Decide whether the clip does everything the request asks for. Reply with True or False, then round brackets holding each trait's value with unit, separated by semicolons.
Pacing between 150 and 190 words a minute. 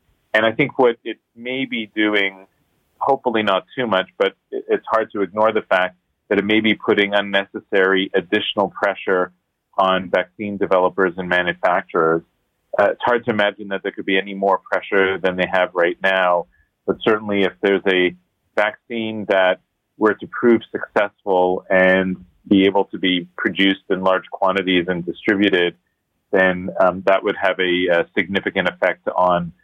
True (165 wpm)